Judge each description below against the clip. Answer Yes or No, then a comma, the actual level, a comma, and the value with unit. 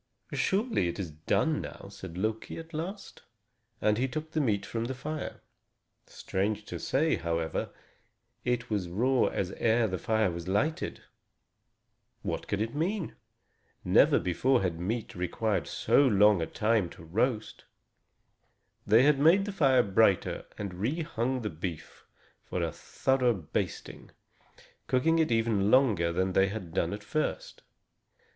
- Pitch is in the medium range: No, low, 110 Hz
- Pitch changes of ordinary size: No, wide, 5.9 semitones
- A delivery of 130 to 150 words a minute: Yes, average, 145 wpm